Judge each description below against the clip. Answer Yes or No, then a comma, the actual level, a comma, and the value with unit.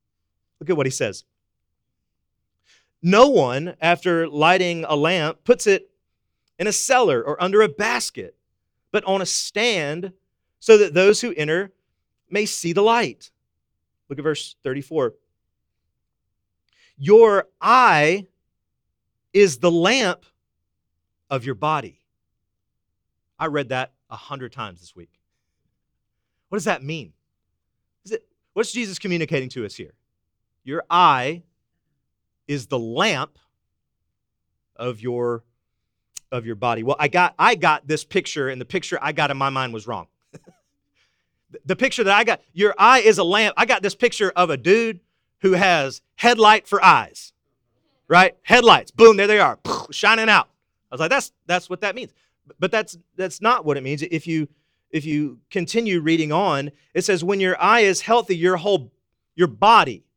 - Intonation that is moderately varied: No, wide, 6.8 semitones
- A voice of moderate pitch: Yes, medium, 170 Hz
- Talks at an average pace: Yes, average, 155 wpm